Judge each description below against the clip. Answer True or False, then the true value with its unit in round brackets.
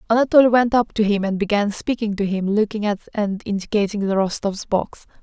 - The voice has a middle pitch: False (210 Hz)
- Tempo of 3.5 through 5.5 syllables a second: False (5.7 syllables/s)